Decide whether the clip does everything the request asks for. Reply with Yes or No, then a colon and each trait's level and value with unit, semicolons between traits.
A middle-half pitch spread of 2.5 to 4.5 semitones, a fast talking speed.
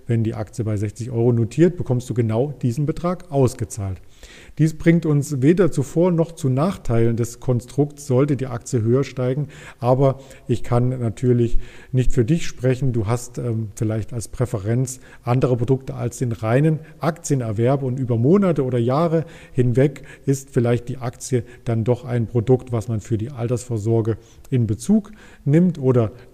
No: average, 3.1 semitones; average, 165 wpm